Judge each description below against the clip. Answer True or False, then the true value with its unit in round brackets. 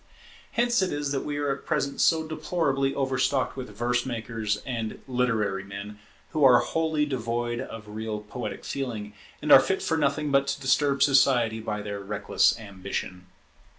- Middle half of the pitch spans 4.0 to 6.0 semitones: True (4.7 semitones)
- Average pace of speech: True (170 wpm)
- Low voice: True (125 Hz)